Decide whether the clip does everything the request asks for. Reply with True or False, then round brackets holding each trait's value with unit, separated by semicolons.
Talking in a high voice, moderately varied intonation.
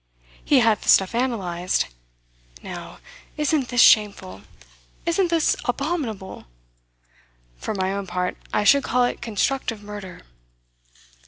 False (225 Hz; 6.0 semitones)